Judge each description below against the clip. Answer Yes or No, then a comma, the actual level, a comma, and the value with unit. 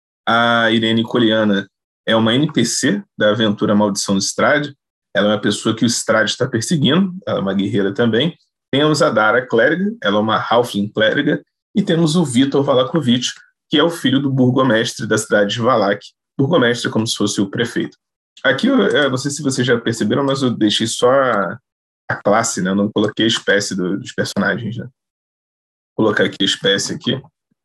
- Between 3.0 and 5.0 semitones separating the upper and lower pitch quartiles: Yes, average, 4.5 semitones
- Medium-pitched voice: No, low, 115 Hz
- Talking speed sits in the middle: No, fast, 190 wpm